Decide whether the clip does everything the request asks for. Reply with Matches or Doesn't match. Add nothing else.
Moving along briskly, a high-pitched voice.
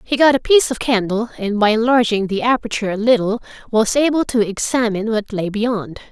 Doesn't match